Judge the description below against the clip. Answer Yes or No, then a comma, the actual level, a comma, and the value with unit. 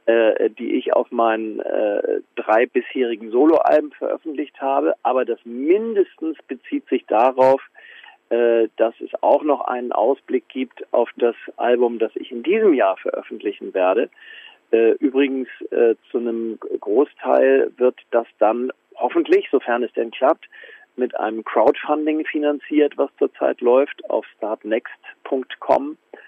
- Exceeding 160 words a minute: No, average, 130 wpm